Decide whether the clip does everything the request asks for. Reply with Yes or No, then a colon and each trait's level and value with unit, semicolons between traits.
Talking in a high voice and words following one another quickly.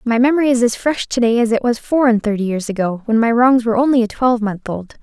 Yes: high, 235 Hz; fast, 275 wpm